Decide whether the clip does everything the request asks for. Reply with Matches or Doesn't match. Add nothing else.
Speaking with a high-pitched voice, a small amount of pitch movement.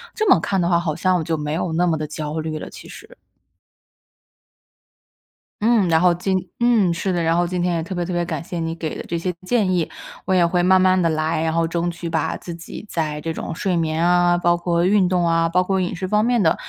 Doesn't match